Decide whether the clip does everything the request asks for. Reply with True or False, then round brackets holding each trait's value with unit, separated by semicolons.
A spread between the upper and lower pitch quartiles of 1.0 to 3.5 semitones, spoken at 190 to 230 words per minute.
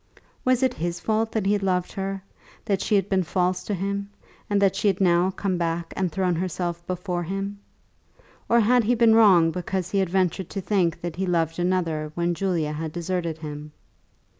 True (2.5 semitones; 200 wpm)